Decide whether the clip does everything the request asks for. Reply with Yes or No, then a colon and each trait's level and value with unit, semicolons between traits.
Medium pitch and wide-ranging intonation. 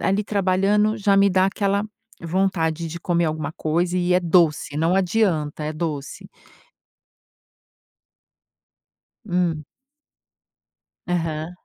No: medium, 175 Hz; average, 3.3 semitones